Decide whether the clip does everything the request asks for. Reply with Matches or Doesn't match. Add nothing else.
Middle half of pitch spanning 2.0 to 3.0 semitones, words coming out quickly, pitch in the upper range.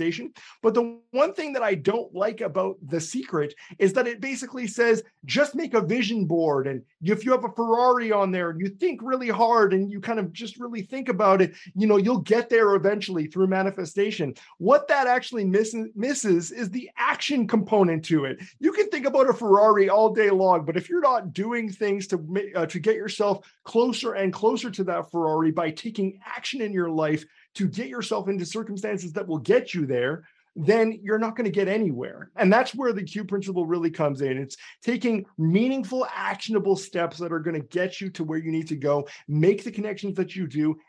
Doesn't match